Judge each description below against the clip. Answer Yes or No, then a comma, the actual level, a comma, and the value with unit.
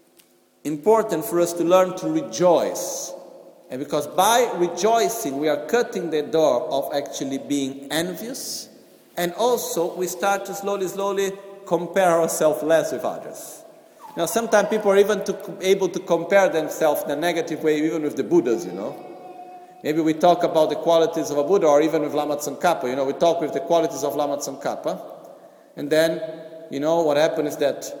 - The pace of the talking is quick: Yes, fast, 180 wpm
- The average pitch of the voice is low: No, medium, 170 Hz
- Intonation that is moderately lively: Yes, average, 4.3 semitones